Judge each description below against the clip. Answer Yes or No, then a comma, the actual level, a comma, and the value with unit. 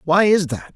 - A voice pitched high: No, medium, 175 Hz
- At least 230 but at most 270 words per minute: Yes, fast, 240 wpm